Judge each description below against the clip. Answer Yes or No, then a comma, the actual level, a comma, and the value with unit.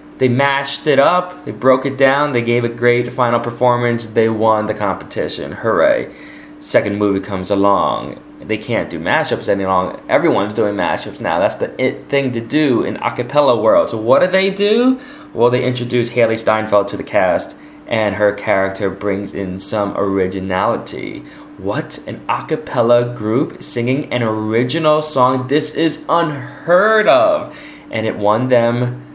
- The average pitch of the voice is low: Yes, low, 120 Hz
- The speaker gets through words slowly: No, average, 165 wpm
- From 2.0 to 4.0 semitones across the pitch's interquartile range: No, average, 5.1 semitones